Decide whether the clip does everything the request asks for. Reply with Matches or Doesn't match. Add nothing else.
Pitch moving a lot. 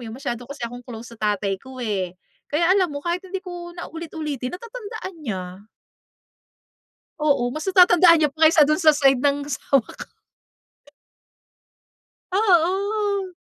Matches